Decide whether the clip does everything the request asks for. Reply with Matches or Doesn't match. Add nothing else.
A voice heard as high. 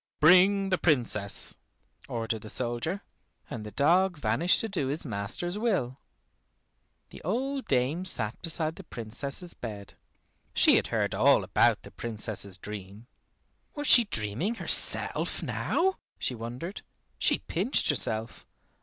Doesn't match